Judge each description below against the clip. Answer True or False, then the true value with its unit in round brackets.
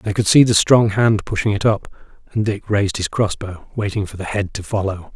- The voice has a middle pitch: False (100 Hz)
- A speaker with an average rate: False (245 wpm)